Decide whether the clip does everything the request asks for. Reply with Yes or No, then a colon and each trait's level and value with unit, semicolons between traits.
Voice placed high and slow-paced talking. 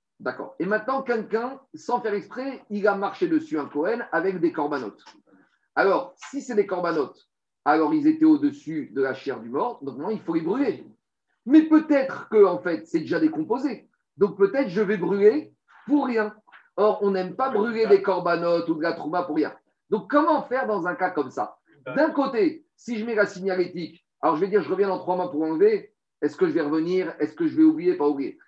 No: high, 215 Hz; average, 215 wpm